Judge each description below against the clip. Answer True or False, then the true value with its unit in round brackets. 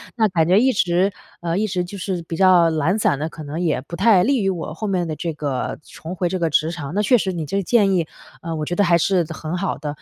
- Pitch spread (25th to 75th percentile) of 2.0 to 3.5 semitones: True (3.2 semitones)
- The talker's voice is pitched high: False (175 Hz)